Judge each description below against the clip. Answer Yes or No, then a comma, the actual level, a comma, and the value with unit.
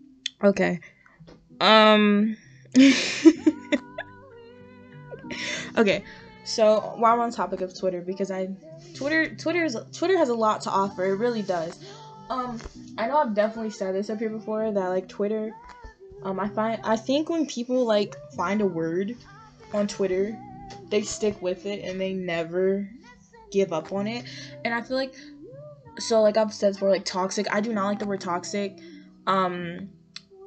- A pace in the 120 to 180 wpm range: Yes, average, 160 wpm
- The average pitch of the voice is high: Yes, high, 205 Hz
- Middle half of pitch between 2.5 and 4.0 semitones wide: Yes, average, 3.7 semitones